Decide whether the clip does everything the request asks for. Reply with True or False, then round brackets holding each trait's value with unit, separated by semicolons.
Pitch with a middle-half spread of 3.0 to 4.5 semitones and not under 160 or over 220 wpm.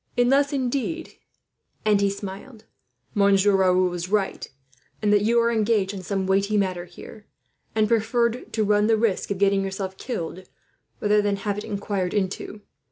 False (2.5 semitones; 165 wpm)